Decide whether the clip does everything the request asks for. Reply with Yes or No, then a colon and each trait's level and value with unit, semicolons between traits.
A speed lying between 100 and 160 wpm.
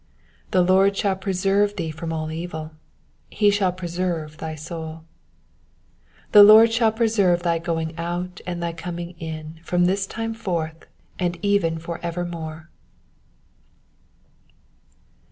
Yes: slow, 135 wpm